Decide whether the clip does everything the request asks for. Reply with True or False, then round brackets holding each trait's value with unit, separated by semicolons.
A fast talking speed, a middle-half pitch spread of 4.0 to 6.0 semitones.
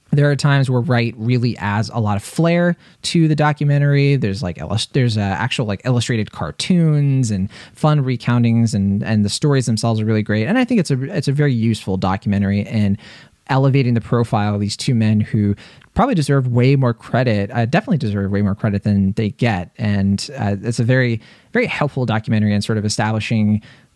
False (195 wpm; 4.9 semitones)